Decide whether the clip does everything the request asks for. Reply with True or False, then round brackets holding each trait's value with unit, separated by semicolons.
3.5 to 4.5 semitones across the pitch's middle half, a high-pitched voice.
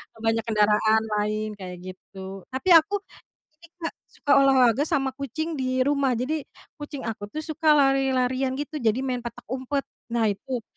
True (4.1 semitones; 255 Hz)